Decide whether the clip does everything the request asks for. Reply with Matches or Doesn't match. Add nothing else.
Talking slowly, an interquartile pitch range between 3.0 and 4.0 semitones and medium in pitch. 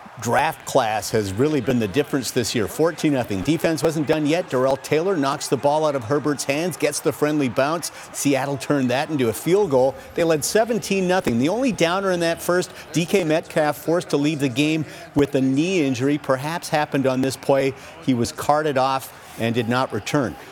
Doesn't match